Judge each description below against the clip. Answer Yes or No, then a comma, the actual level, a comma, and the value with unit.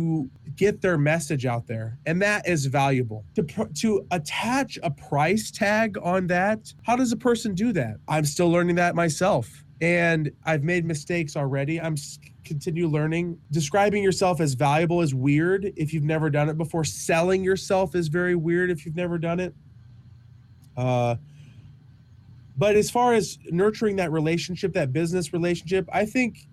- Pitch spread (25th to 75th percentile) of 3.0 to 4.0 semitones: No, average, 4.5 semitones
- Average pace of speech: Yes, average, 165 wpm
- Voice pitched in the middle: Yes, medium, 165 Hz